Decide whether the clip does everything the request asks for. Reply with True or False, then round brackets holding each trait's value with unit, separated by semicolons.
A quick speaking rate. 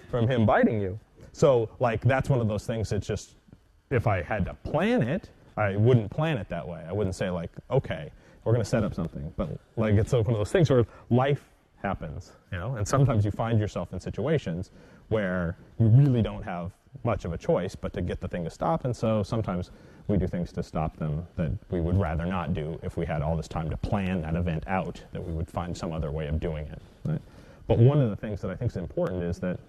True (240 wpm)